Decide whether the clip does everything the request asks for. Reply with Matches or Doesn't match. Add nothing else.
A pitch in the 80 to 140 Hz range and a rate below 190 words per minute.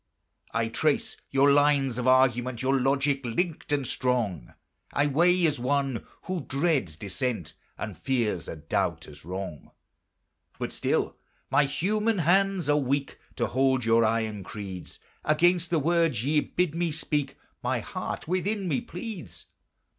Matches